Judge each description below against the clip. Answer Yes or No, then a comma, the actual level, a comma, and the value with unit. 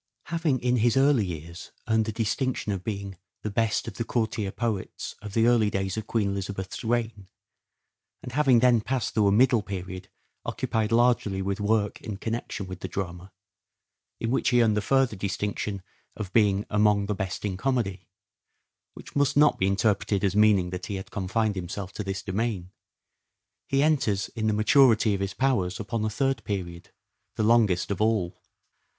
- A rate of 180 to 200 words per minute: Yes, average, 185 wpm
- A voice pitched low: Yes, low, 105 Hz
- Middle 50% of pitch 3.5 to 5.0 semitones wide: No, average, 3.1 semitones